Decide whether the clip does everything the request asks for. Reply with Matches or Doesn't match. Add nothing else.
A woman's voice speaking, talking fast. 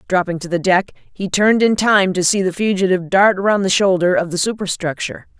Matches